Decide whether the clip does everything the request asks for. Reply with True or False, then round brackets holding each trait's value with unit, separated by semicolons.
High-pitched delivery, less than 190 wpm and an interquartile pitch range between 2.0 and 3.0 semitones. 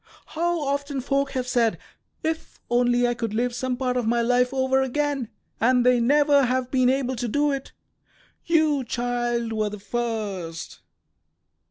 True (250 Hz; 160 wpm; 2.5 semitones)